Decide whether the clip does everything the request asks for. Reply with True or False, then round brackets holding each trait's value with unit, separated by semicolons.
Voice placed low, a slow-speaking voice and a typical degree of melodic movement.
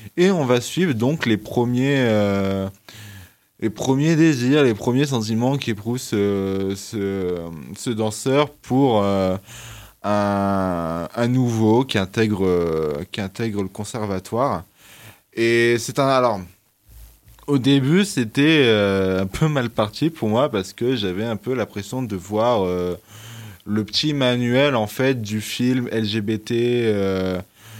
True (110 Hz; 140 wpm; 4.2 semitones)